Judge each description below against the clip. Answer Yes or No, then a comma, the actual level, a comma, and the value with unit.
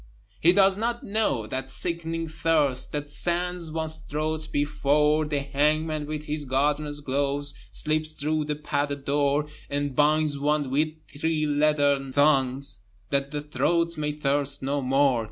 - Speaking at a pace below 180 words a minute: Yes, average, 145 wpm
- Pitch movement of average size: No, narrow, 1.7 semitones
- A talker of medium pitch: Yes, medium, 150 Hz